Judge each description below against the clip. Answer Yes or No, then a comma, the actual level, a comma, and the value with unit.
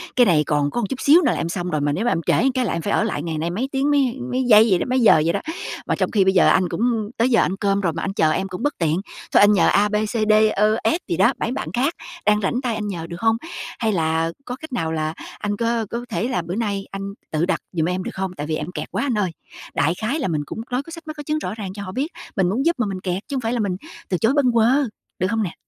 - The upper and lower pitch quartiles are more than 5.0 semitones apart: Yes, wide, 5.6 semitones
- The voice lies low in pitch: No, high, 205 Hz